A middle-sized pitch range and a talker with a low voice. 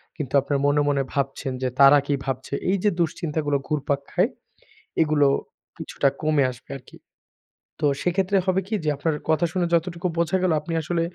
No: average, 3.6 semitones; medium, 155 Hz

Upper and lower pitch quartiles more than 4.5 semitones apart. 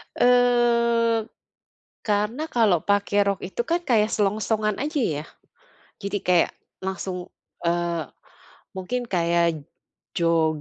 Yes: average, 4.9 semitones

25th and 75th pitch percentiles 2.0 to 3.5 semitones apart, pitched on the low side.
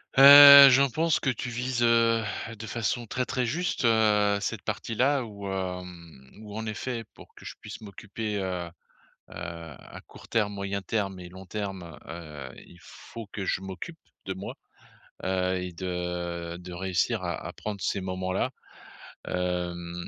No: average, 4.3 semitones; low, 100 Hz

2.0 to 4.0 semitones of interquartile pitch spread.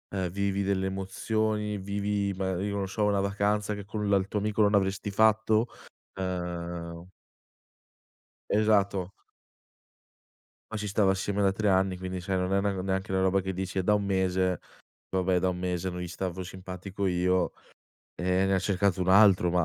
No: narrow, 1.6 semitones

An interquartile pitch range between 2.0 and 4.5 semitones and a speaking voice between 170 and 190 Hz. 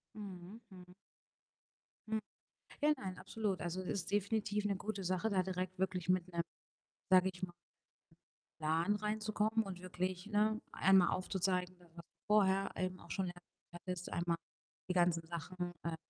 Yes: narrow, 2.4 semitones; medium, 185 Hz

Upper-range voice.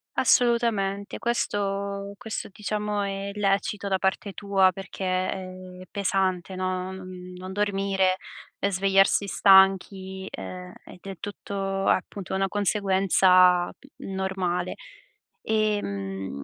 Yes: high, 195 Hz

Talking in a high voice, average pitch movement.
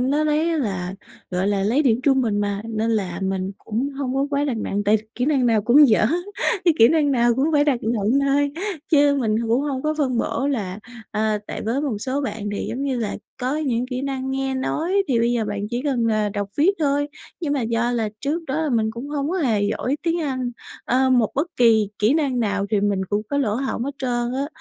Yes: very high, 250 Hz; average, 4.5 semitones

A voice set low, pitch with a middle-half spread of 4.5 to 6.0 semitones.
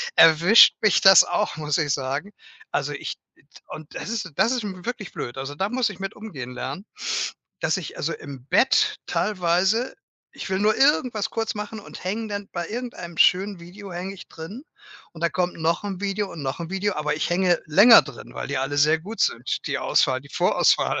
No: medium, 185 Hz; average, 5.2 semitones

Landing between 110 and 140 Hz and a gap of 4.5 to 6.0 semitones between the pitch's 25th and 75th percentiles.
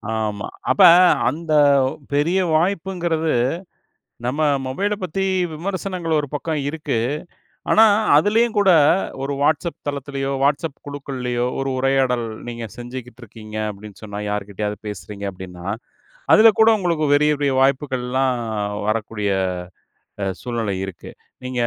Yes: low, 135 Hz; wide, 5.6 semitones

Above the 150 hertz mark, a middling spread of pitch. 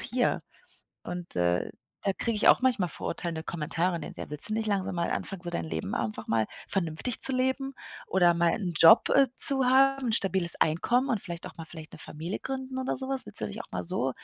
No: medium, 185 Hz; wide, 7.6 semitones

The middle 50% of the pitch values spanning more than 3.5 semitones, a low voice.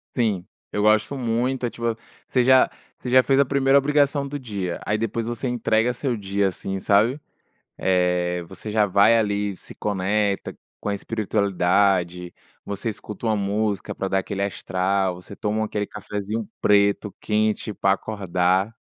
No: average, 2.9 semitones; low, 105 Hz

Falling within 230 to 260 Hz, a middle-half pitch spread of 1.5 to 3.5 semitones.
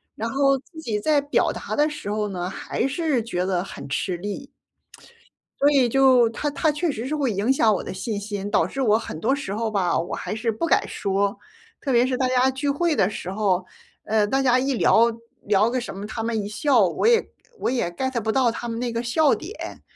No: high, 235 Hz; average, 4.8 semitones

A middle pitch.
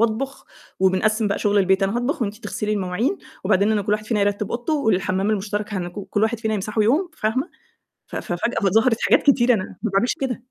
No: high, 215 Hz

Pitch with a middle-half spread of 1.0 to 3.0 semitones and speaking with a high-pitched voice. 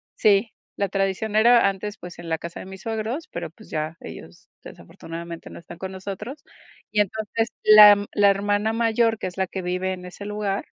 Yes: average, 2.7 semitones; high, 200 Hz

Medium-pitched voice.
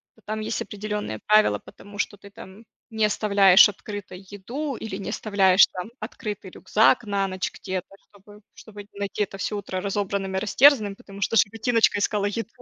No: high, 205 Hz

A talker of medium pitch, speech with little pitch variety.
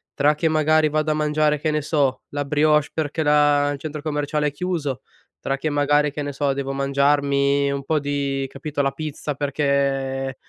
Yes: medium, 145 Hz; narrow, 1.5 semitones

